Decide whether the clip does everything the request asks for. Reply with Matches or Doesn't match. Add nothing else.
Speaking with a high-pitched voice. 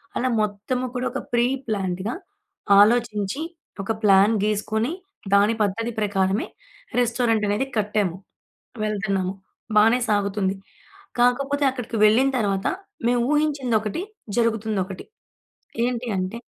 Matches